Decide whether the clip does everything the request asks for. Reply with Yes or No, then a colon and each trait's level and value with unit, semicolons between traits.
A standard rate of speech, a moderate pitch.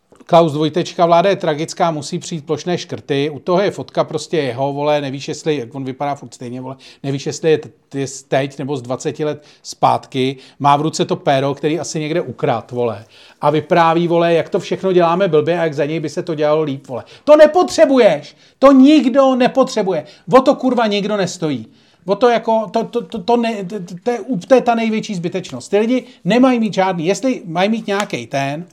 No: fast, 180 wpm; medium, 165 Hz